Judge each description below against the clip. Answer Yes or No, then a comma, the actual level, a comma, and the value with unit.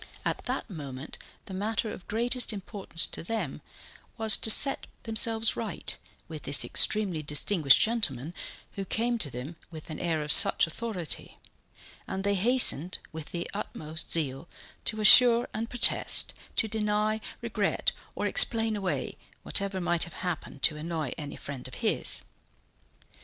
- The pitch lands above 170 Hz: Yes, high, 190 Hz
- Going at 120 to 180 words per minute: Yes, average, 145 wpm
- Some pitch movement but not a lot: No, wide, 5.9 semitones